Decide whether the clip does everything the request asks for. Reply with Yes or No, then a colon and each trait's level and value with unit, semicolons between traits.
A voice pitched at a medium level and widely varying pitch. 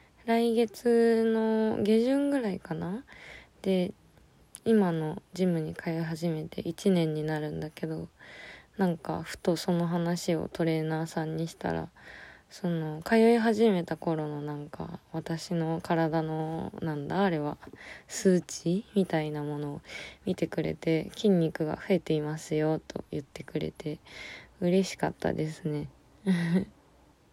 No: medium, 165 Hz; average, 3.7 semitones